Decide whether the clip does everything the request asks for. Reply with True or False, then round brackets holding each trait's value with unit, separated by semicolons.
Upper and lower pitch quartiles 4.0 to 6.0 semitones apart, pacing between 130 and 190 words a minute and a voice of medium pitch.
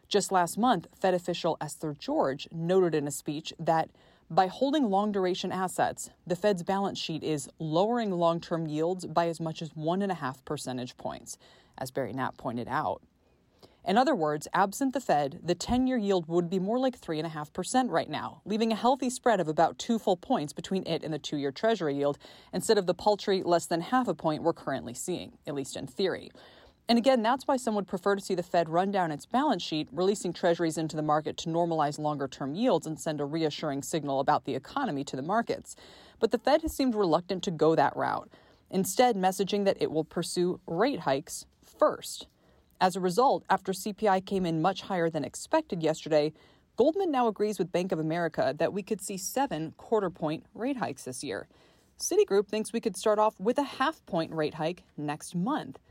False (5.1 semitones; 205 wpm; 180 Hz)